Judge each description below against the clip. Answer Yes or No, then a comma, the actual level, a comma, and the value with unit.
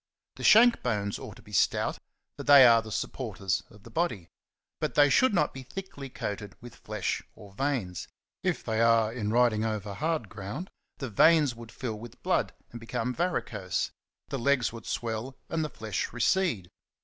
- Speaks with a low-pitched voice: Yes, low, 115 Hz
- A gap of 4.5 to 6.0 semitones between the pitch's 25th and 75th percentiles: Yes, average, 4.9 semitones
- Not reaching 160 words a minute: No, average, 180 wpm